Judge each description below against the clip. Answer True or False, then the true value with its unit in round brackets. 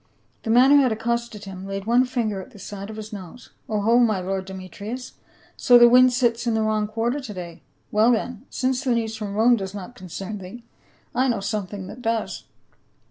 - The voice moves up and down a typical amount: True (3.4 semitones)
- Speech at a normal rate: False (215 wpm)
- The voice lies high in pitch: True (220 Hz)